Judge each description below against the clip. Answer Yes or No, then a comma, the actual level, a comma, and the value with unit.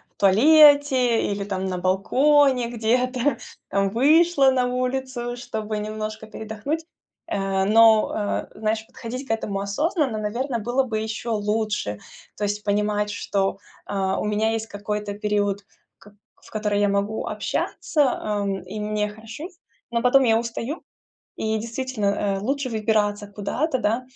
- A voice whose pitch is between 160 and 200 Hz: No, high, 220 Hz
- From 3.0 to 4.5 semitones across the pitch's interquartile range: Yes, average, 3.3 semitones